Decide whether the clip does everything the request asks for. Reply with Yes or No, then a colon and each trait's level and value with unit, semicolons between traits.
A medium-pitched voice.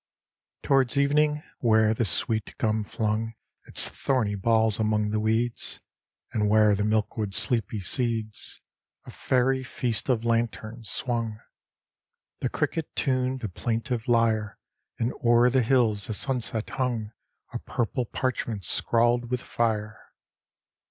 No: low, 115 Hz